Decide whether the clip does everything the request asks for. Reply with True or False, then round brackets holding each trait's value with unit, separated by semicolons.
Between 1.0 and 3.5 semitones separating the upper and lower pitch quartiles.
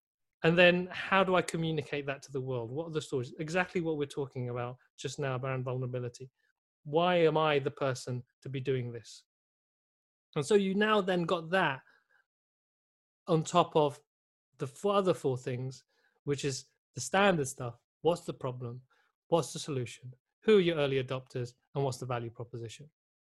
False (4.7 semitones)